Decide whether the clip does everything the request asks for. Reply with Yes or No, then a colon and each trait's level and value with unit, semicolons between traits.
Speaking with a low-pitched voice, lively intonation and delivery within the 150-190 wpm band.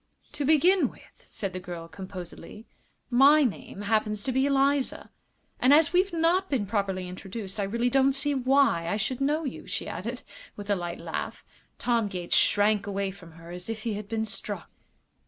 No: high, 220 Hz; wide, 6.0 semitones; average, 185 wpm